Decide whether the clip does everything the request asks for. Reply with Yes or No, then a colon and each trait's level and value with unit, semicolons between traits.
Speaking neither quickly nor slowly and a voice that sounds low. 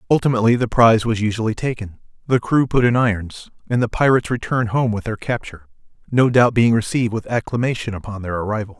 Yes: average, 190 wpm; low, 115 Hz